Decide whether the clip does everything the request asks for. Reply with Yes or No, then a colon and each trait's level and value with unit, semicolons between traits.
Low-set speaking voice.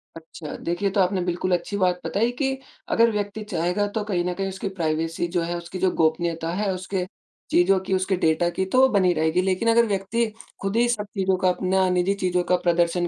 No: medium, 185 Hz